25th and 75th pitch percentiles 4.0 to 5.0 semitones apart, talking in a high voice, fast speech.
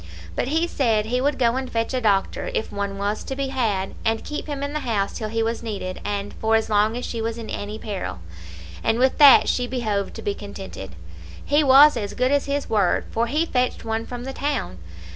Yes: average, 4.4 semitones; high, 230 Hz; fast, 230 wpm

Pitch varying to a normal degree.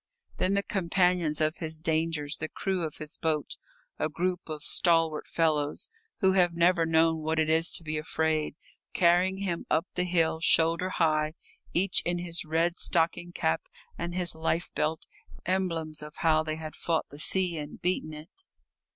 No: narrow, 2.1 semitones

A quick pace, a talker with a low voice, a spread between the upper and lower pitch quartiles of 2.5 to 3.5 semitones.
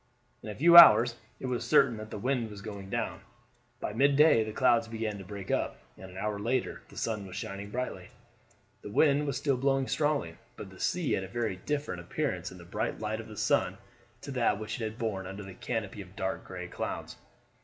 No: fast, 220 wpm; low, 110 Hz; average, 4.6 semitones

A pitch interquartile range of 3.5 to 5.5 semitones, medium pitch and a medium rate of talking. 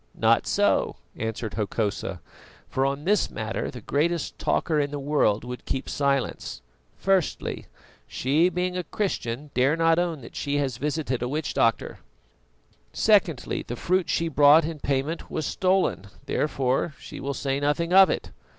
Yes: average, 4.2 semitones; medium, 145 Hz; average, 155 wpm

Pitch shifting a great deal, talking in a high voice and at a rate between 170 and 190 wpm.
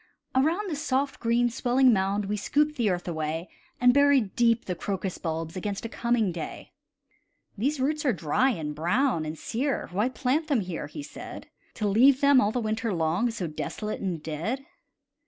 Yes: wide, 6.6 semitones; high, 225 Hz; average, 180 wpm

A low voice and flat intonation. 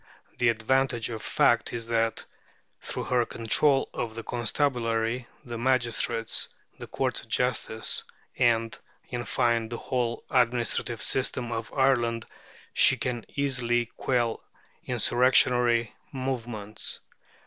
Yes: low, 120 Hz; narrow, 1.6 semitones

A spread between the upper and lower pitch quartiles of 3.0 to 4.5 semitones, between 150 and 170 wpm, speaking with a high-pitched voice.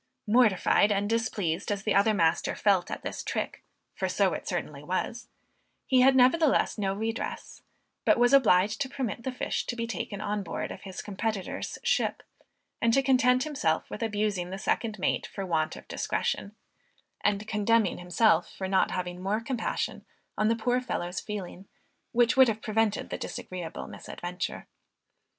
Yes: average, 3.5 semitones; average, 165 wpm; high, 210 Hz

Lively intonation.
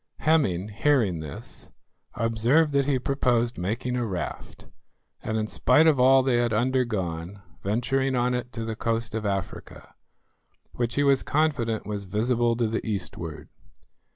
No: average, 3.7 semitones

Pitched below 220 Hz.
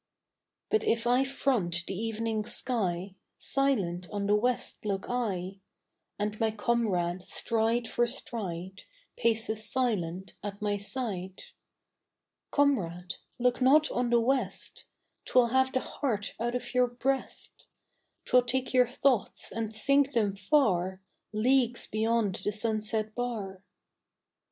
No: high, 225 Hz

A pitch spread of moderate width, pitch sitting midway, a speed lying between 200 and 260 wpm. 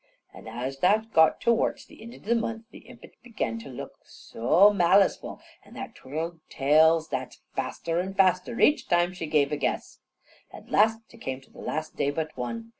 No: wide, 7.1 semitones; medium, 170 Hz; fast, 205 wpm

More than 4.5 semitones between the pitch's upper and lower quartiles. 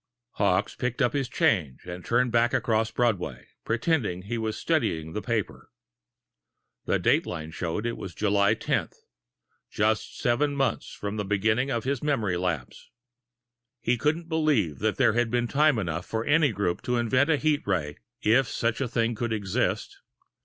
No: average, 4.2 semitones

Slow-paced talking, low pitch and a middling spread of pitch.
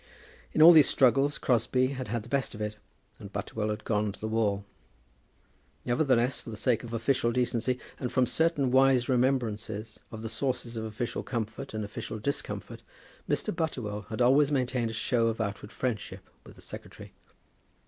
No: average, 175 wpm; low, 120 Hz; average, 3.1 semitones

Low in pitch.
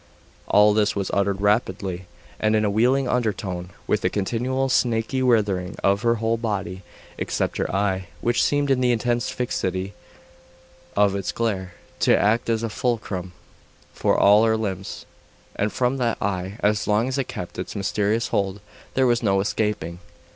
Yes: low, 105 Hz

